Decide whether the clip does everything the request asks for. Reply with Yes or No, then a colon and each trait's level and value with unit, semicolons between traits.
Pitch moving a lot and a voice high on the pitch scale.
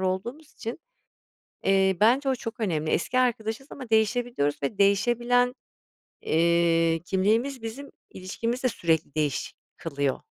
Yes: wide, 6.4 semitones; high, 220 Hz